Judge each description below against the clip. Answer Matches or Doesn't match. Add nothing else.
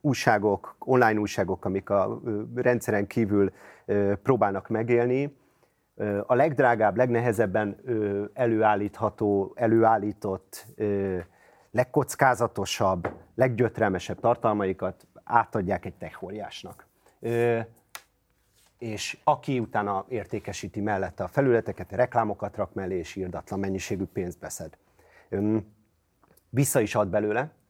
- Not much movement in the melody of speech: Doesn't match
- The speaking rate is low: Matches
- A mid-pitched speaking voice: Doesn't match